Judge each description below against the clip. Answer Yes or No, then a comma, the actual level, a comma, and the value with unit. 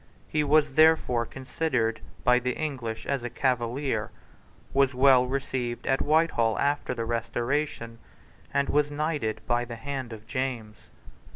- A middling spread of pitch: Yes, average, 3.3 semitones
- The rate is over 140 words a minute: No, slow, 135 wpm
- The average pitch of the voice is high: No, low, 130 Hz